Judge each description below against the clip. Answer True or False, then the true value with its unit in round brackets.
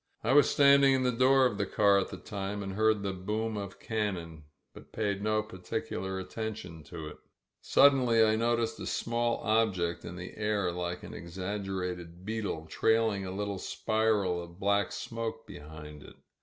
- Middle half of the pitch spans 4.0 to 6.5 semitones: False (3.5 semitones)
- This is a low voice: True (100 Hz)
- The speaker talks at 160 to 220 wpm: True (180 wpm)